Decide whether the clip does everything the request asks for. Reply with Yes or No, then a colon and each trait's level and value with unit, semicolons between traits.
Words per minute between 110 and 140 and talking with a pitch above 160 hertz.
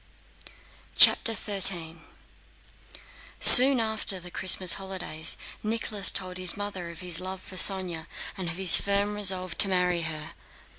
Yes: slow, 135 wpm; medium, 185 Hz